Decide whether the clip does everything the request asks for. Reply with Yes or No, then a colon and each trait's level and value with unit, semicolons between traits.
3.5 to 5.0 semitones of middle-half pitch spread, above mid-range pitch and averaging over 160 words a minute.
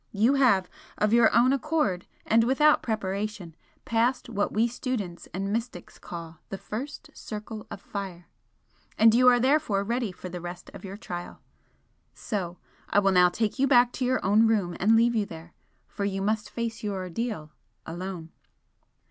Yes: average, 4.2 semitones; high, 210 Hz; average, 170 wpm